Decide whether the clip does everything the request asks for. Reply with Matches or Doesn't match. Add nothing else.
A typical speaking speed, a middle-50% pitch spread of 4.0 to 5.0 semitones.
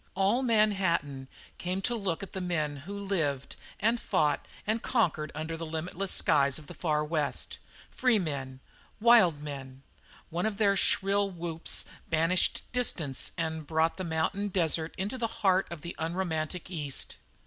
Matches